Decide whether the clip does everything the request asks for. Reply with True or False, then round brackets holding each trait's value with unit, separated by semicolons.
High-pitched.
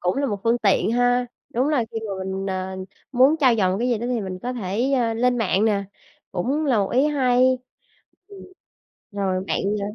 True (235 Hz)